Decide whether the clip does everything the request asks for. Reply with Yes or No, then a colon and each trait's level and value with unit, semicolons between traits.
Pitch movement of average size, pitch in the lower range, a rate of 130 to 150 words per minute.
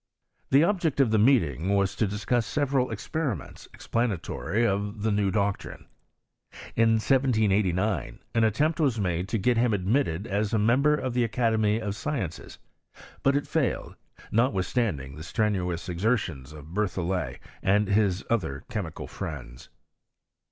Yes: average, 4.5 semitones; low, 105 Hz; average, 140 wpm